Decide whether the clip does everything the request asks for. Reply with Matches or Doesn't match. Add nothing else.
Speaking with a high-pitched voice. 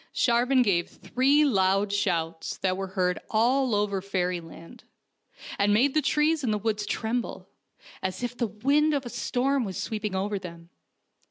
Matches